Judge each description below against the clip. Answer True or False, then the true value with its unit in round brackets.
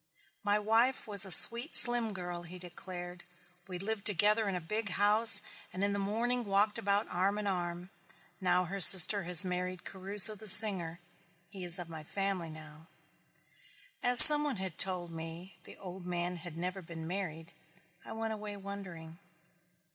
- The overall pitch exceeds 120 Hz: True (190 Hz)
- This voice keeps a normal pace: True (170 wpm)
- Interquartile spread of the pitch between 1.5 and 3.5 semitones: True (2.9 semitones)